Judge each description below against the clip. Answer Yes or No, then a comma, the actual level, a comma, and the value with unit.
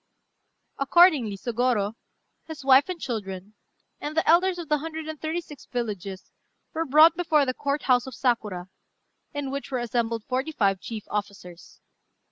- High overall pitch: Yes, very high, 260 Hz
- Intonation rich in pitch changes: Yes, wide, 6.3 semitones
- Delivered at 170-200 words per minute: No, average, 155 wpm